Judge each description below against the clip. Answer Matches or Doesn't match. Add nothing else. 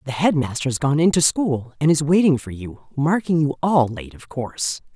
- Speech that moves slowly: Doesn't match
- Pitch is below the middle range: Doesn't match